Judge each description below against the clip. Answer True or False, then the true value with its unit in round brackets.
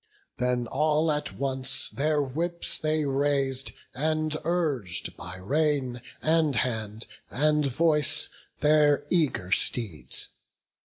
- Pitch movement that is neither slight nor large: True (3.6 semitones)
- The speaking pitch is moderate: True (145 Hz)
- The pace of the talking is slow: True (105 wpm)